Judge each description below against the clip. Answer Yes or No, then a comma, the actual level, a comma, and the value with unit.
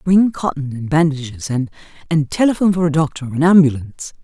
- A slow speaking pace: No, average, 155 wpm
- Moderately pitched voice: Yes, medium, 155 Hz